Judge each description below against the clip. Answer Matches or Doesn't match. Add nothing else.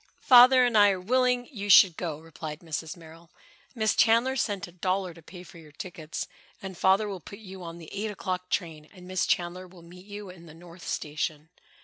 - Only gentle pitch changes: Doesn't match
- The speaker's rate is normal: Doesn't match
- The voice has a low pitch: Doesn't match